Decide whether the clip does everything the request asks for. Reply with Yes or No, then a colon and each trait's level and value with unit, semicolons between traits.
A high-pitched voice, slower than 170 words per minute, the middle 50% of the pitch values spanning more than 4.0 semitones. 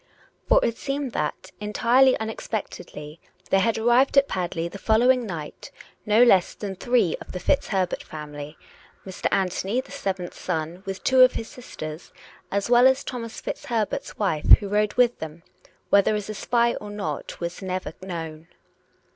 Yes: high, 205 Hz; average, 160 wpm; average, 5.2 semitones